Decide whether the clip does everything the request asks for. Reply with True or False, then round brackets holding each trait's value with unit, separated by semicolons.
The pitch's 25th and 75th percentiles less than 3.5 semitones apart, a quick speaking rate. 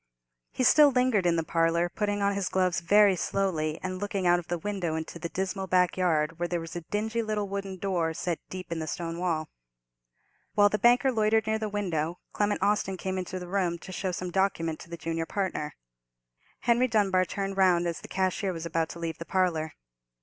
True (3.1 semitones; 210 wpm)